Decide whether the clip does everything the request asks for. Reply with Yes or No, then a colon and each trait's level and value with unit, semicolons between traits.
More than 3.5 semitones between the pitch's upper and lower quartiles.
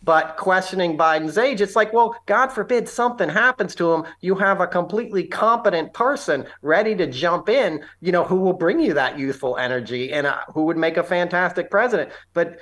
Yes: average, 3.9 semitones